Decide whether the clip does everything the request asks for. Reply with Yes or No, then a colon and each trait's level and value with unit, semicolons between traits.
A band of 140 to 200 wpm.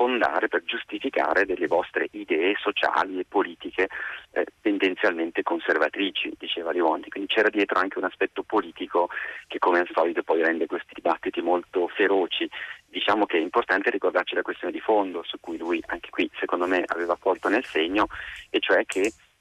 Yes: average, 165 wpm